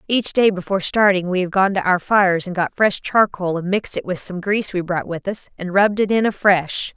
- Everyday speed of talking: No, fast, 250 wpm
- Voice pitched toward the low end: No, high, 190 Hz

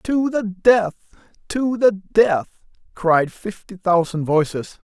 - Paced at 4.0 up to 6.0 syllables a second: No, 3.4 syllables/s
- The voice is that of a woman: No, male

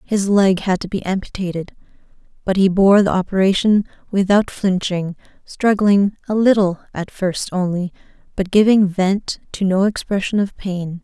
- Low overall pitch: No, high, 195 Hz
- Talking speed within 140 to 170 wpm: Yes, average, 145 wpm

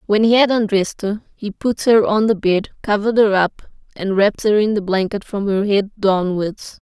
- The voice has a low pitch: No, high, 205 Hz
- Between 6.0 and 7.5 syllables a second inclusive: No, 5.1 syllables/s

